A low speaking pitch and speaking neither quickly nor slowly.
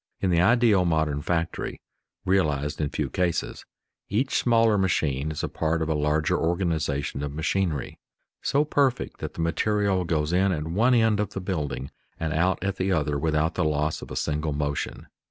Yes: very low, 85 Hz; average, 180 wpm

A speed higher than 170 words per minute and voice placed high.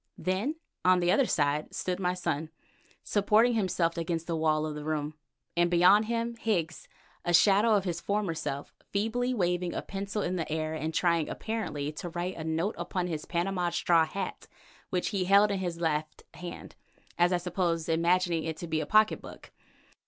No: average, 185 wpm; medium, 175 Hz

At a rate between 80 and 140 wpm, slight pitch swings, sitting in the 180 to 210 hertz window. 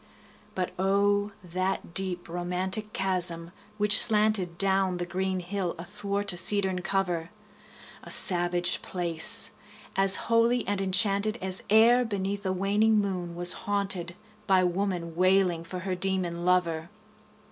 Yes: slow, 135 wpm; narrow, 2.2 semitones; high, 190 Hz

